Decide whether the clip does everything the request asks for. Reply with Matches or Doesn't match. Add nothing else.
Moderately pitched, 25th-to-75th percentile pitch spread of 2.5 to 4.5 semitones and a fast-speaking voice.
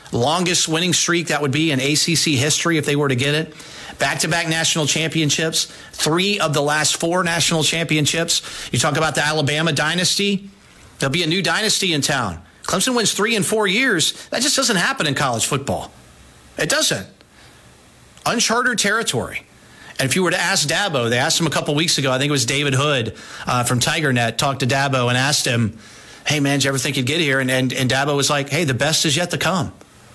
Matches